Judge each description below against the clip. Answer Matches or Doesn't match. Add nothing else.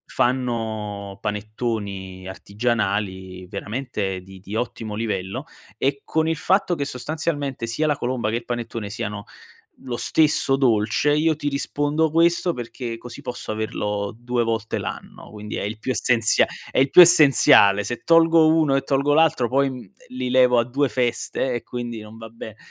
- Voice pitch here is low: Matches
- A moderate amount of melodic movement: Matches